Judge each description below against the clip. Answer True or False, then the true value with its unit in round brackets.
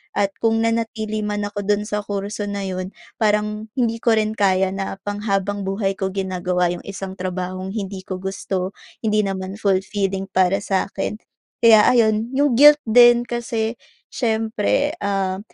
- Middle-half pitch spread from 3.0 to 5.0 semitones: False (2.4 semitones)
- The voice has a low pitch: False (205 Hz)